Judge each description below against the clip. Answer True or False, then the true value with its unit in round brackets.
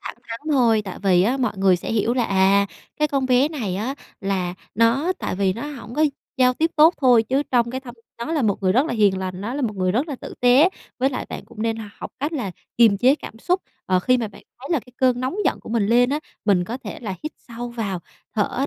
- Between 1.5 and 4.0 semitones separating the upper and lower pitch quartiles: False (4.8 semitones)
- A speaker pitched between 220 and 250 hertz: True (235 Hz)